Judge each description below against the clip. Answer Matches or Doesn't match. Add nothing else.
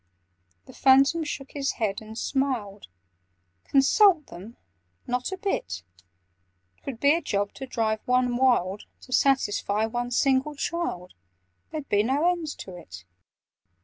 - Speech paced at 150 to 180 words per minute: Doesn't match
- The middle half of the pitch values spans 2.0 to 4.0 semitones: Doesn't match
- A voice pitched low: Doesn't match